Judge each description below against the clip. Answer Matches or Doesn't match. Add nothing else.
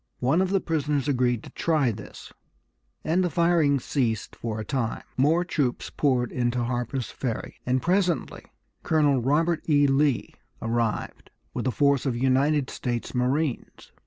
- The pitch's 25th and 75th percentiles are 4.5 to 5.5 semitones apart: Doesn't match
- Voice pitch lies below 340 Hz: Matches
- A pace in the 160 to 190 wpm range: Doesn't match